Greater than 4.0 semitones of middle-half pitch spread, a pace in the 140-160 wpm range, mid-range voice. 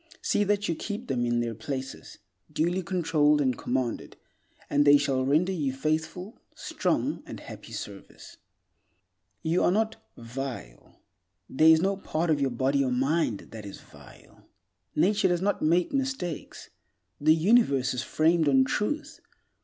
Yes: wide, 5.4 semitones; average, 150 wpm; medium, 155 Hz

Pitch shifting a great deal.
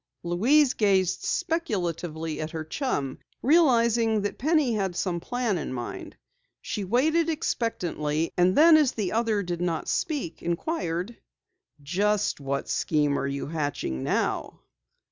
Yes: wide, 7.2 semitones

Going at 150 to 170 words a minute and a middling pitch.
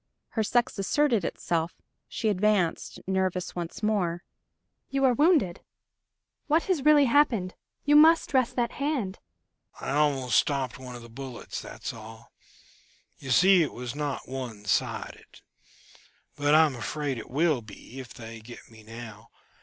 Yes: average, 155 wpm; medium, 165 Hz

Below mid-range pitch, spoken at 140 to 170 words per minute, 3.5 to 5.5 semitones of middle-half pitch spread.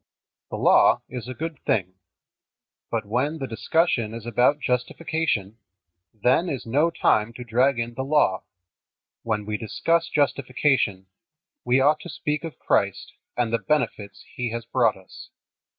Yes: low, 125 Hz; average, 150 wpm; average, 4.9 semitones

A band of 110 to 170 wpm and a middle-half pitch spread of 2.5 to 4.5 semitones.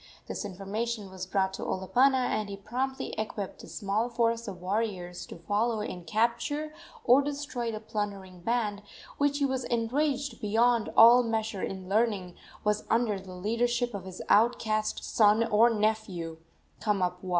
Yes: average, 150 wpm; average, 3.4 semitones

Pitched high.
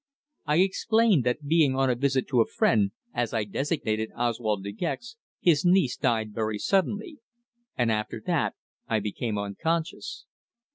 No: low, 125 Hz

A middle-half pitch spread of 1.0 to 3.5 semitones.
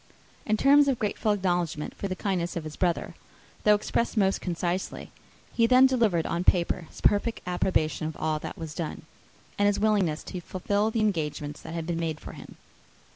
No: average, 4.2 semitones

